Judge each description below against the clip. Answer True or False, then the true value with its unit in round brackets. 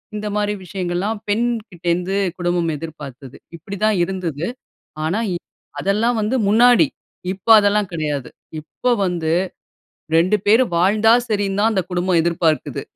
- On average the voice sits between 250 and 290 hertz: False (190 Hz)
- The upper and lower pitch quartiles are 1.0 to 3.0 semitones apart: False (3.8 semitones)